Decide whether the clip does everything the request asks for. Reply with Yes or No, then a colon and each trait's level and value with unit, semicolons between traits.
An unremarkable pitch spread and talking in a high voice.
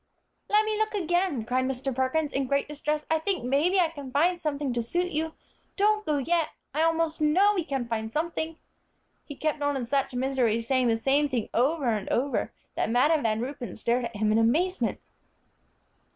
Yes: average, 4.7 semitones; very high, 285 Hz